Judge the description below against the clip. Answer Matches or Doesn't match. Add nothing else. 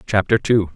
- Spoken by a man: Matches